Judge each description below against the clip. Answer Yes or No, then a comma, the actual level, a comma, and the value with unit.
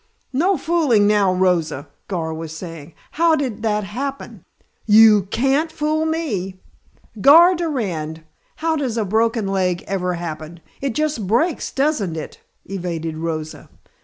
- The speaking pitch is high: Yes, high, 210 Hz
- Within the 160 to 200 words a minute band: No, slow, 135 wpm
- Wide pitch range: Yes, wide, 8.4 semitones